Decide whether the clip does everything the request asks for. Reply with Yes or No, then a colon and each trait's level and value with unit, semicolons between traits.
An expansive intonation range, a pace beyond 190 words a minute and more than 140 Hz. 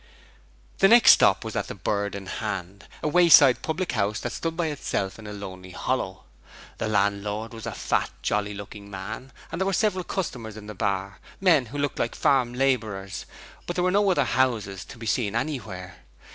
No: wide, 6.4 semitones; average, 200 wpm; low, 110 Hz